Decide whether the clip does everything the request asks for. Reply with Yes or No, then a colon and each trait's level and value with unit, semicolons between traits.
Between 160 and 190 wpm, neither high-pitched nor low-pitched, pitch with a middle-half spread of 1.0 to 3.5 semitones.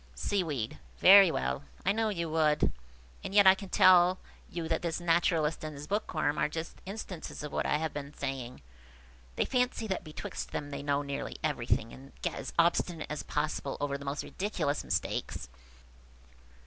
No: average, 175 wpm; medium, 155 Hz; average, 4.4 semitones